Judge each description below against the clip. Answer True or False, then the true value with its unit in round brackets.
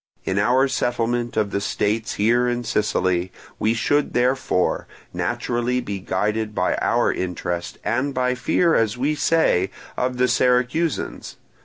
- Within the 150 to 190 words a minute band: False (140 wpm)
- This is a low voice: True (120 Hz)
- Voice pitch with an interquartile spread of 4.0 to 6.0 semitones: False (3.4 semitones)